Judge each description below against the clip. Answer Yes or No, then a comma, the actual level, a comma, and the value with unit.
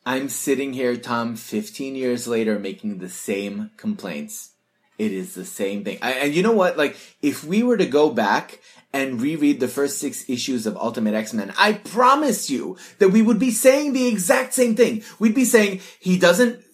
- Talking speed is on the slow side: No, average, 195 wpm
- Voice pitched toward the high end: No, medium, 175 Hz